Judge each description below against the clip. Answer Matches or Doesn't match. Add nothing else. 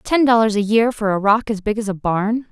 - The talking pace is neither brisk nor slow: Doesn't match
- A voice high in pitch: Matches